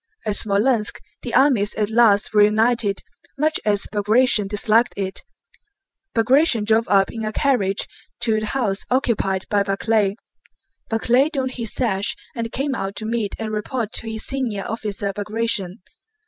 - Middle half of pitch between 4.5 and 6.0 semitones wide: No, average, 2.8 semitones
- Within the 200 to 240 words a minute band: No, average, 145 wpm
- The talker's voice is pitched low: No, high, 220 Hz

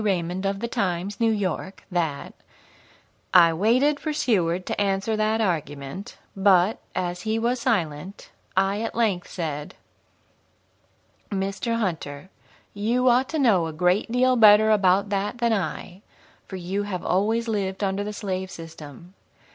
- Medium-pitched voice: No, high, 195 Hz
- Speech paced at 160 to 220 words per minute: No, average, 145 wpm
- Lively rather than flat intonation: No, average, 3.7 semitones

